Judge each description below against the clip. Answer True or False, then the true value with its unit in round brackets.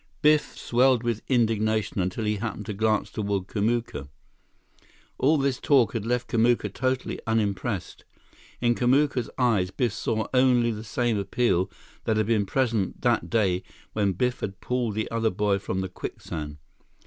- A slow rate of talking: False (155 wpm)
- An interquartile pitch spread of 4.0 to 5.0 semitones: False (3.4 semitones)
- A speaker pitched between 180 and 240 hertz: False (110 Hz)